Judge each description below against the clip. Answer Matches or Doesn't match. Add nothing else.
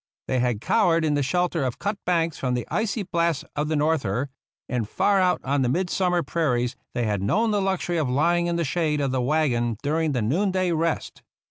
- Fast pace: Matches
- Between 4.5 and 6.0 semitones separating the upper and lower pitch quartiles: Matches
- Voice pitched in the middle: Matches